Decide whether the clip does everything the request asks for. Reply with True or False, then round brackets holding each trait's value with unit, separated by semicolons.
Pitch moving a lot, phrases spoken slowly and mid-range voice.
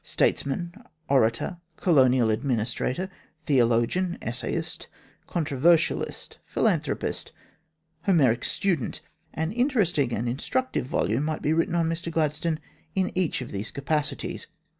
True (5.8 semitones; 105 wpm; 150 Hz)